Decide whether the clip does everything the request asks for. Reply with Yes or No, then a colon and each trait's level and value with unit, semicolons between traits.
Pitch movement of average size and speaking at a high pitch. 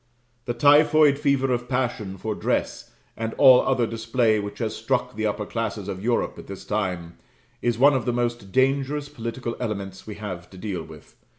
No: average, 4.2 semitones; low, 115 Hz